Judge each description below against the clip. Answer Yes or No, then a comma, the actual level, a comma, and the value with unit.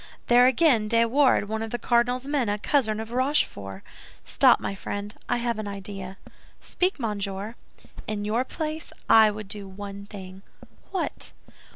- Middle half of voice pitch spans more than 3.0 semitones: Yes, average, 3.5 semitones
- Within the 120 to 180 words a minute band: Yes, average, 160 wpm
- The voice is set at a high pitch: Yes, high, 220 Hz